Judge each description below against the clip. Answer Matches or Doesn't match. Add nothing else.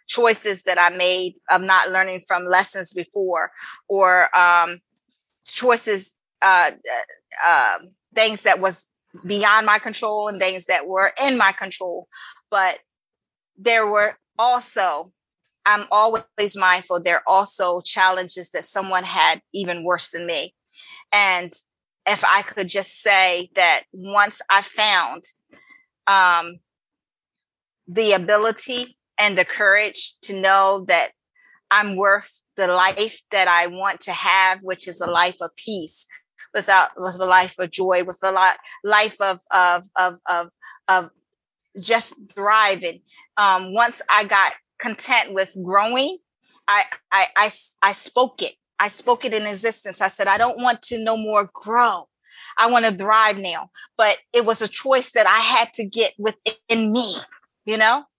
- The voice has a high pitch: Matches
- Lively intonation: Doesn't match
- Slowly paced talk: Doesn't match